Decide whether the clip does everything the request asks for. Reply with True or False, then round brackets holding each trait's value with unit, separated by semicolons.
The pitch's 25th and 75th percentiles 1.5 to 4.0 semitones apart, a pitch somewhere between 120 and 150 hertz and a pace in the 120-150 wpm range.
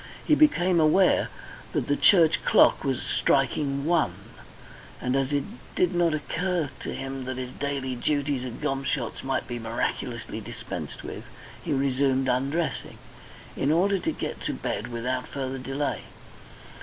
True (3.4 semitones; 140 Hz; 145 wpm)